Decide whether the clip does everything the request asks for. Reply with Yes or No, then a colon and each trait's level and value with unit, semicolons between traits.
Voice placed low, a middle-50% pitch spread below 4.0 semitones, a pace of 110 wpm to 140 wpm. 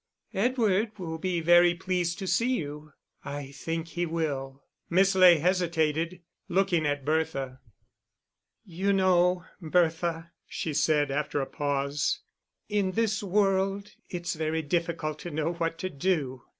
No: medium, 170 Hz; average, 3.4 semitones; slow, 135 wpm